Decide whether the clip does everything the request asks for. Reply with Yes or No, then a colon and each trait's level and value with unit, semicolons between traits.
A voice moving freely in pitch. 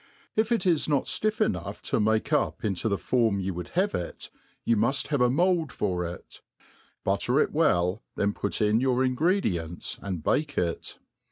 Yes: wide, 7.6 semitones